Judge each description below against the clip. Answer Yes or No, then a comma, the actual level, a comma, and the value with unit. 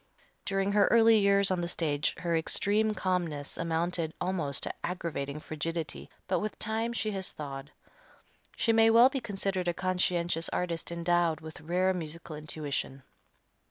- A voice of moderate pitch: Yes, medium, 175 Hz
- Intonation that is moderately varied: Yes, average, 3.8 semitones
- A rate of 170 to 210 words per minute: No, average, 150 wpm